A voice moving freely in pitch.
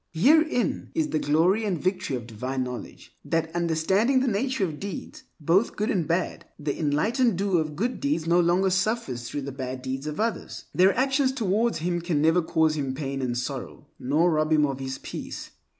Yes: wide, 6.0 semitones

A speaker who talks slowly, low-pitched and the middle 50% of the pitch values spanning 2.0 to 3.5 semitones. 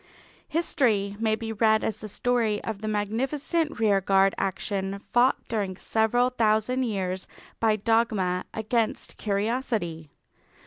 No: slow, 120 wpm; high, 220 Hz; average, 2.8 semitones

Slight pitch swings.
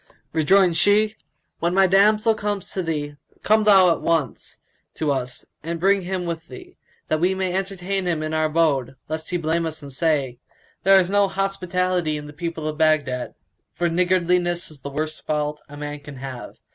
No: average, 3.8 semitones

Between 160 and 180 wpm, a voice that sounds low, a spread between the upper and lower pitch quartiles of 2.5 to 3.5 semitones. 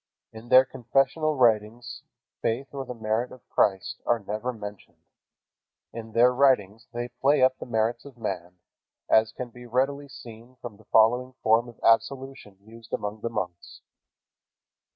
No: average, 150 wpm; low, 120 Hz; average, 2.8 semitones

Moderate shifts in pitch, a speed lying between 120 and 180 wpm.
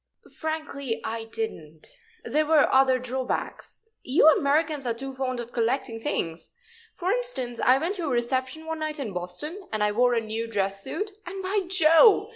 No: wide, 5.7 semitones; average, 175 wpm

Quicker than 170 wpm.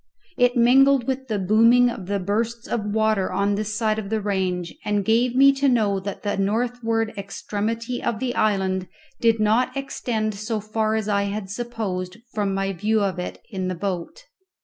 Yes: average, 180 wpm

